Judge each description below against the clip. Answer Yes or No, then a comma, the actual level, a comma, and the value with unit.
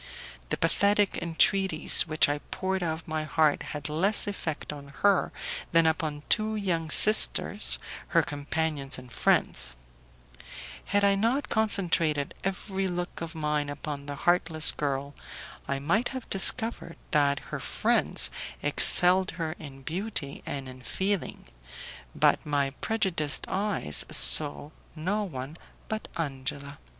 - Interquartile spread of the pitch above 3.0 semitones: Yes, average, 5.1 semitones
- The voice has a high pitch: No, medium, 160 Hz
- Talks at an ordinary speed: No, slow, 130 wpm